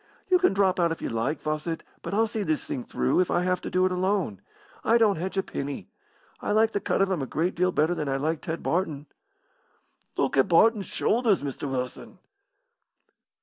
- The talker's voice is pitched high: No, medium, 180 Hz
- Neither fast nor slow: No, fast, 210 wpm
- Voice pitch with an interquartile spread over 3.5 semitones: Yes, average, 4.5 semitones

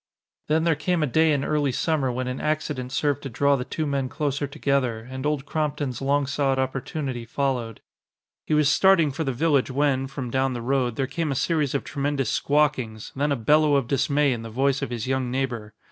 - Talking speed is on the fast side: Yes, fast, 210 wpm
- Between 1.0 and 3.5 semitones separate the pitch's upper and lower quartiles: Yes, narrow, 2.5 semitones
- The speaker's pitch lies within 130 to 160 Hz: Yes, medium, 140 Hz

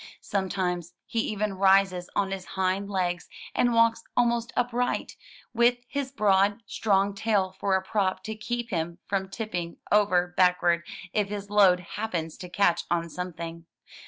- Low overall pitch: No, high, 195 Hz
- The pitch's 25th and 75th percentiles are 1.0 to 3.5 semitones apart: Yes, average, 3.1 semitones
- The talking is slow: No, average, 155 wpm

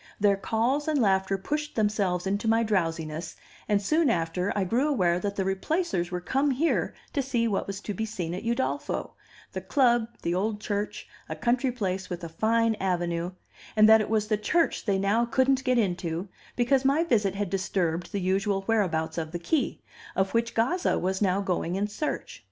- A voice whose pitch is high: Yes, high, 205 Hz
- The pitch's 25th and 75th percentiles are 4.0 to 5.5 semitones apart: Yes, average, 4.4 semitones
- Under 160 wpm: No, average, 190 wpm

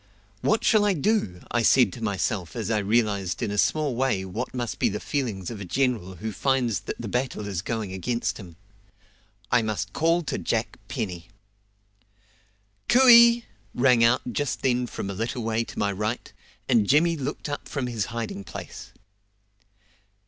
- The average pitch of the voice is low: Yes, low, 115 Hz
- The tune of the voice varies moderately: Yes, average, 4.6 semitones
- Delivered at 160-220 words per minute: Yes, average, 170 wpm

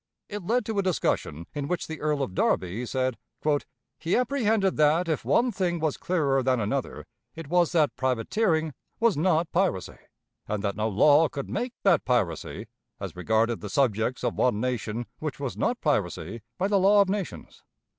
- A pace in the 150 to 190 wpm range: Yes, average, 175 wpm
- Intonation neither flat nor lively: No, wide, 7.9 semitones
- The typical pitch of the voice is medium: Yes, medium, 150 Hz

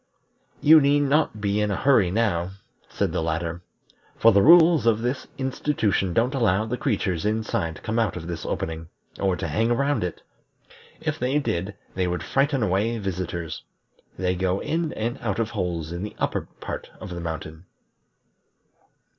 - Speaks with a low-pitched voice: Yes, low, 105 Hz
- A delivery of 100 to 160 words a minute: No, average, 170 wpm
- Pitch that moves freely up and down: Yes, wide, 5.9 semitones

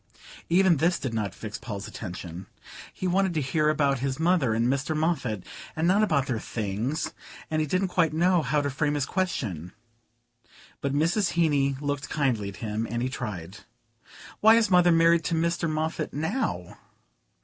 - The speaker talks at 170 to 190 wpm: Yes, average, 175 wpm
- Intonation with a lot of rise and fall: Yes, wide, 6.2 semitones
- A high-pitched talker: No, medium, 150 Hz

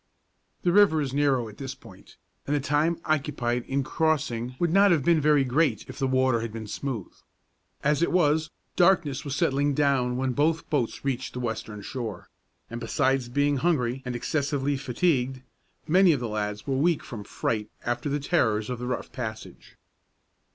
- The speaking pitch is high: No, low, 135 Hz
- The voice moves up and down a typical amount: Yes, average, 3.8 semitones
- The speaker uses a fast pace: No, average, 180 wpm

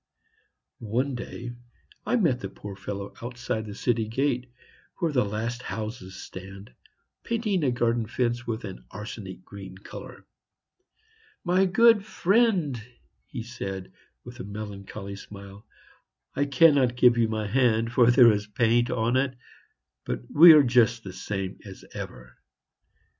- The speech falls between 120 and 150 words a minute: Yes, average, 140 wpm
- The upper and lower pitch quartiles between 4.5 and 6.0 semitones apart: No, average, 4.0 semitones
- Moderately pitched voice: No, low, 120 Hz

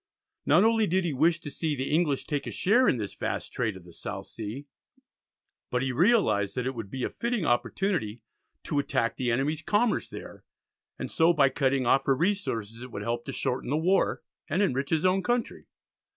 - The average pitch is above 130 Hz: Yes, medium, 140 Hz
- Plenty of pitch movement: Yes, wide, 6.5 semitones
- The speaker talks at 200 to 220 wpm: Yes, fast, 205 wpm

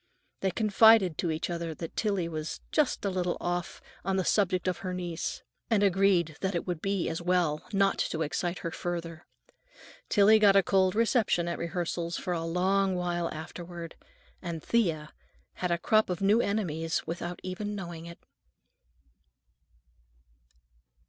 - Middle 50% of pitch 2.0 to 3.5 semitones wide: Yes, narrow, 2.6 semitones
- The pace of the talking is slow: No, average, 155 wpm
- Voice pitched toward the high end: No, medium, 180 Hz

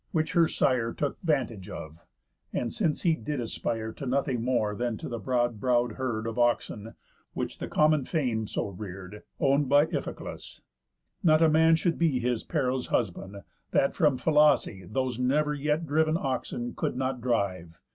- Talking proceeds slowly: No, average, 165 wpm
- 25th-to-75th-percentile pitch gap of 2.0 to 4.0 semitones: No, average, 4.9 semitones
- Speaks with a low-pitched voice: Yes, low, 125 Hz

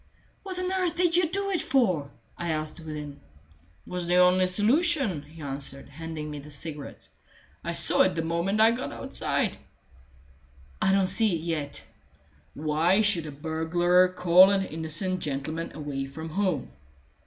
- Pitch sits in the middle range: Yes, medium, 170 Hz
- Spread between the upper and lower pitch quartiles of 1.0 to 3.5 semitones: No, average, 4.4 semitones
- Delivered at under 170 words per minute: Yes, average, 160 wpm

